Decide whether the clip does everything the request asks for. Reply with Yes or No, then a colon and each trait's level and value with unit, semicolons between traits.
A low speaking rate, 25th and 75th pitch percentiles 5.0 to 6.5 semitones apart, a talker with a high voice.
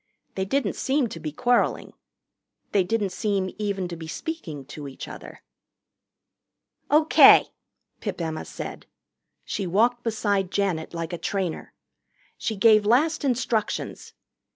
Yes: slow, 130 wpm; average, 5.3 semitones; high, 200 Hz